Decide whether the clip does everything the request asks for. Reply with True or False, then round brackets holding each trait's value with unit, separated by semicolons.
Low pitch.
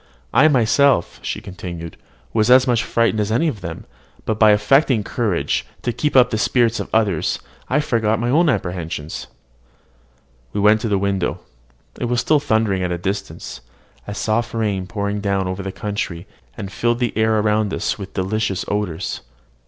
True (105 Hz)